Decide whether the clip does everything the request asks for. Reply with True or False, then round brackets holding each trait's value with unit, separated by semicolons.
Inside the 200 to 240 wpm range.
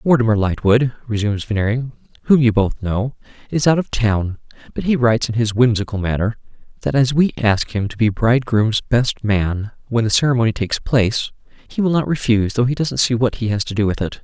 True (205 wpm)